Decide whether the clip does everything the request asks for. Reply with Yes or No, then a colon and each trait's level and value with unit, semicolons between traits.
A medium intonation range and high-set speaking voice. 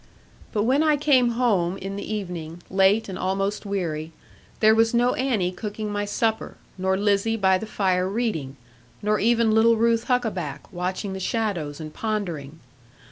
Yes: average, 3.6 semitones; high, 205 Hz